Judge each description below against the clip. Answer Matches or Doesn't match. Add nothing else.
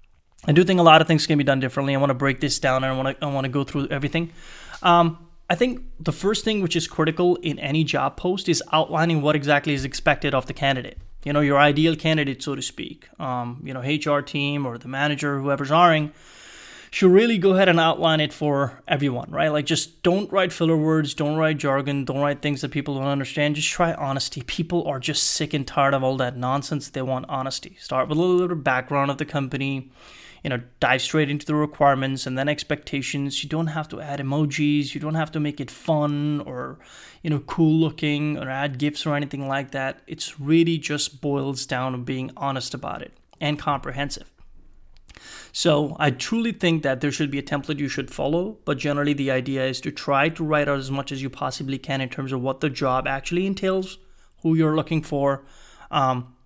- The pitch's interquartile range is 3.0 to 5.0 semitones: Doesn't match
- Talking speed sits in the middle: Doesn't match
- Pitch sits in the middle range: Matches